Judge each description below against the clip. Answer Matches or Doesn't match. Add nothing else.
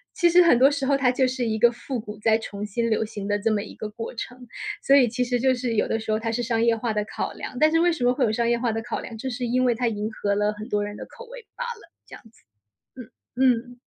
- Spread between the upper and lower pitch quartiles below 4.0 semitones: Matches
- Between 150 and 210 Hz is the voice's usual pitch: Doesn't match